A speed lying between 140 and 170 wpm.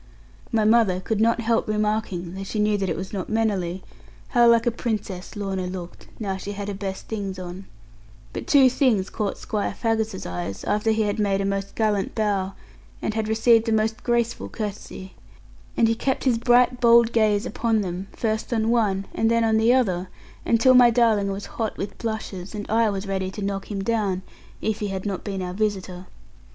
No: average, 195 wpm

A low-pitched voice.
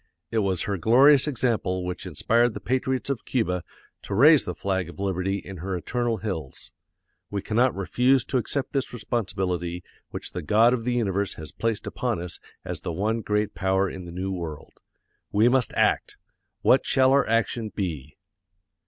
Yes: low, 105 Hz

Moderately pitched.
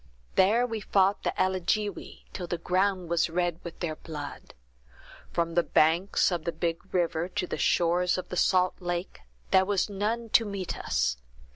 Yes: medium, 180 Hz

